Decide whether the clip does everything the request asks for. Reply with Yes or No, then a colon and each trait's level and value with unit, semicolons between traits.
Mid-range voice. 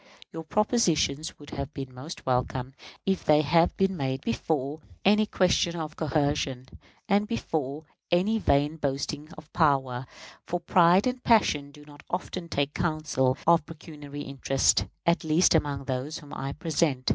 Yes: medium, 150 Hz